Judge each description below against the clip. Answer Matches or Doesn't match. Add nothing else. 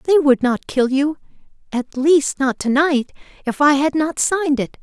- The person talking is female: Matches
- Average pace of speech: Matches